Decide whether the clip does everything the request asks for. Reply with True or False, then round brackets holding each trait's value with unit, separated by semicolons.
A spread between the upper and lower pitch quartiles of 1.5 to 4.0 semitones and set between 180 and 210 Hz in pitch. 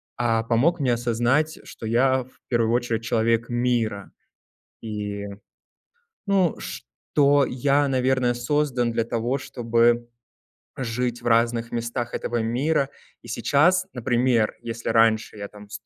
False (2.4 semitones; 120 Hz)